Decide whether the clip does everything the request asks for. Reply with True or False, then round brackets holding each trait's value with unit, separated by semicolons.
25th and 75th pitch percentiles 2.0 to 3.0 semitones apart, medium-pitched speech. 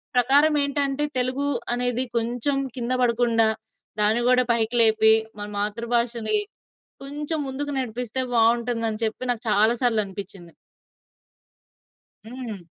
False (2.7 semitones; 240 Hz)